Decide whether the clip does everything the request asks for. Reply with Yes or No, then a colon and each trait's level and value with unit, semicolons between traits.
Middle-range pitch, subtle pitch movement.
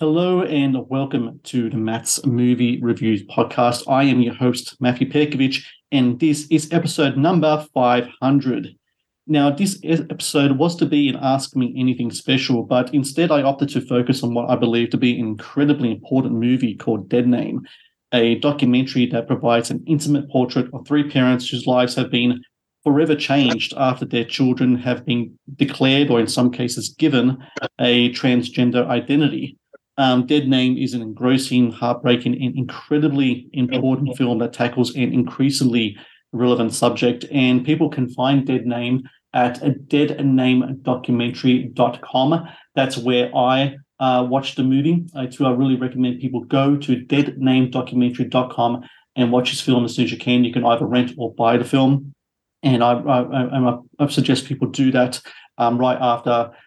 No: low, 130 Hz; narrow, 2.1 semitones